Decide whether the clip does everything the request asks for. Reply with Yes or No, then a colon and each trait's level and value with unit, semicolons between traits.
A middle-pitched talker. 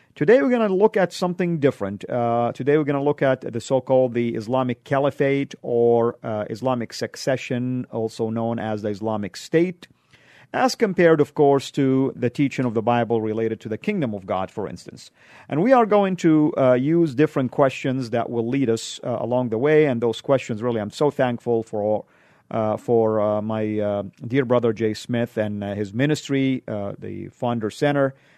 No: low, 125 Hz